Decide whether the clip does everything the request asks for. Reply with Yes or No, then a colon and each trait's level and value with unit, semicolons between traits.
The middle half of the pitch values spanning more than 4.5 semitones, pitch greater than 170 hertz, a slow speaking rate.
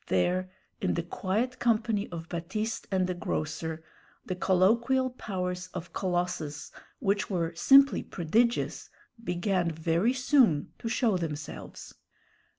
Yes: average, 5.0 semitones; medium, 185 Hz; slow, 120 wpm